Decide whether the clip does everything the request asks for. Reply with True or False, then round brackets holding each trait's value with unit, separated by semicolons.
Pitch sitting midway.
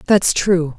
True (175 Hz)